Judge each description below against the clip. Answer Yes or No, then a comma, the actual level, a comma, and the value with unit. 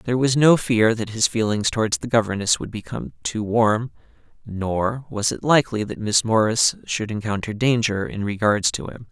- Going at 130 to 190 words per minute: Yes, average, 180 wpm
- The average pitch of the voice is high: No, low, 110 Hz